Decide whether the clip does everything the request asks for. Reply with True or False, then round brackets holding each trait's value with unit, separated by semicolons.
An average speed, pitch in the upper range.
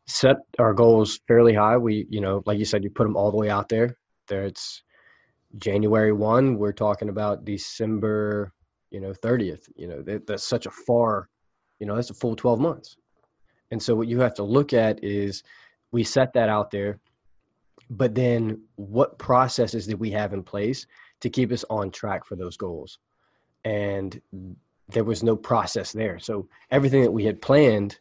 False (185 wpm; 110 Hz)